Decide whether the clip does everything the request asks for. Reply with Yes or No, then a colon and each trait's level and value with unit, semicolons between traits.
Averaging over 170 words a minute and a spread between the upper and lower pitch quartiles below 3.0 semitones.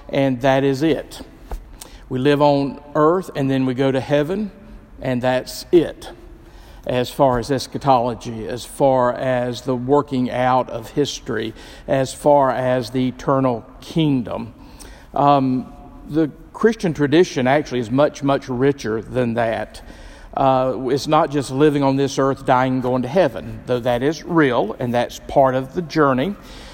No: average, 155 wpm; narrow, 2.4 semitones